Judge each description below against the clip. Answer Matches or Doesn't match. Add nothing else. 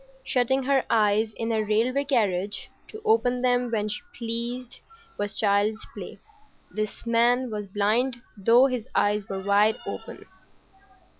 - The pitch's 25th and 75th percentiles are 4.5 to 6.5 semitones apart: Doesn't match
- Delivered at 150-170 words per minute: Doesn't match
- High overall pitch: Matches